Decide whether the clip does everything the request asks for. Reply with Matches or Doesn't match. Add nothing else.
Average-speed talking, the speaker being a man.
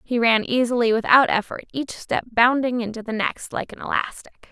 Doesn't match